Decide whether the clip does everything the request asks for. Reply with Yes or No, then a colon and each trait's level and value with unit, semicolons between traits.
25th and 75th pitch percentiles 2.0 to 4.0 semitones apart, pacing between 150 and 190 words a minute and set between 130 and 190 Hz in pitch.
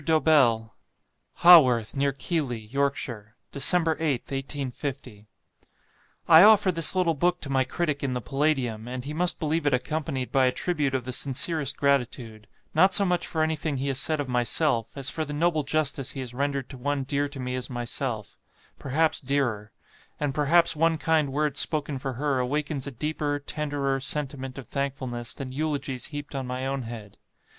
Yes: average, 3.2 semitones; average, 175 wpm; medium, 140 Hz